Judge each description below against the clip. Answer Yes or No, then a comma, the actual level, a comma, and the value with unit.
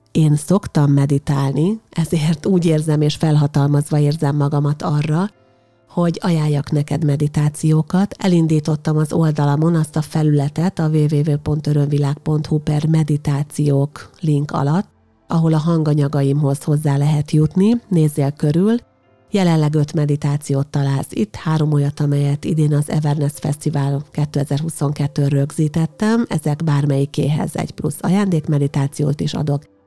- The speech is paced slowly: No, average, 115 wpm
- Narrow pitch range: Yes, narrow, 1.8 semitones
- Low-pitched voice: No, medium, 150 Hz